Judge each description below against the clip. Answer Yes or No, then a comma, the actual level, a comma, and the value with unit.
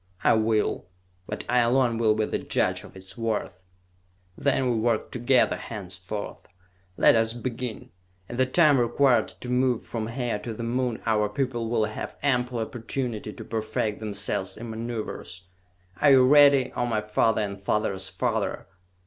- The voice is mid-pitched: No, low, 115 Hz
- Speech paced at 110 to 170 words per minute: Yes, average, 160 wpm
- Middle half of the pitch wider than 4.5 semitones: No, narrow, 2.6 semitones